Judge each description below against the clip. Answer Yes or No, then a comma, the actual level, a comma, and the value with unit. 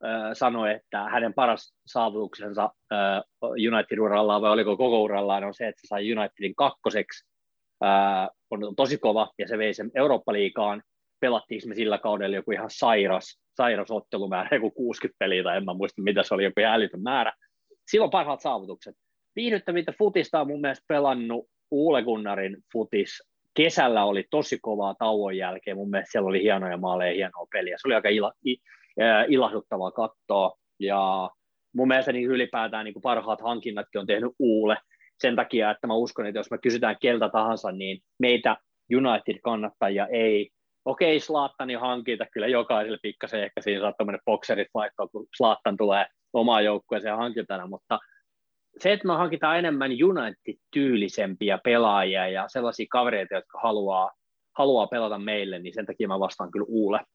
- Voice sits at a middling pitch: No, low, 110 Hz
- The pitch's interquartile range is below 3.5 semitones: No, average, 4.0 semitones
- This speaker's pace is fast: Yes, fast, 160 wpm